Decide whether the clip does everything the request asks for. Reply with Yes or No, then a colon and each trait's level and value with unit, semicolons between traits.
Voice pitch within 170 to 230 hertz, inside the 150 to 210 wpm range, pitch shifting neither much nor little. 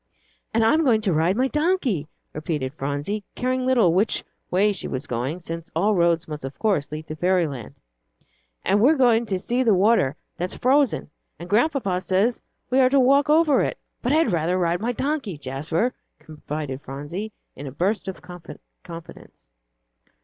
No: medium, 185 Hz; average, 170 wpm; wide, 7.7 semitones